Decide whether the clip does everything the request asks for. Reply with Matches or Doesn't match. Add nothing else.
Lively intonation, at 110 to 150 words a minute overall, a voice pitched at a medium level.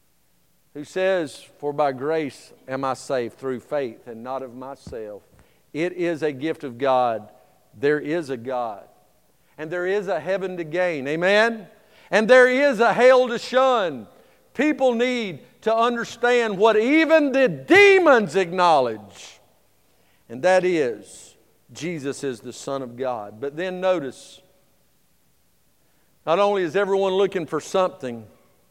Matches